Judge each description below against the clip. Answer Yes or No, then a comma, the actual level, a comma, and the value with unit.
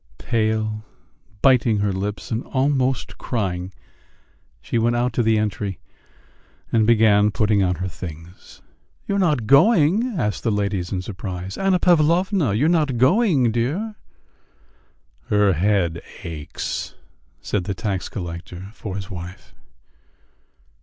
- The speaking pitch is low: Yes, low, 110 Hz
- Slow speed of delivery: Yes, slow, 130 wpm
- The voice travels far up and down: Yes, wide, 5.7 semitones